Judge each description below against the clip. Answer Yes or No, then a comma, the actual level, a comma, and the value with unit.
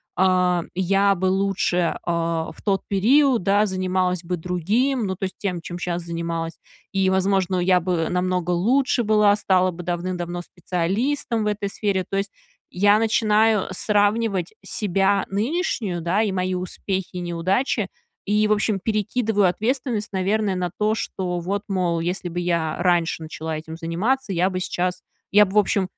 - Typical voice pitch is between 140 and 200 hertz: Yes, high, 190 Hz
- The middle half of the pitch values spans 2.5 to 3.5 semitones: Yes, average, 2.9 semitones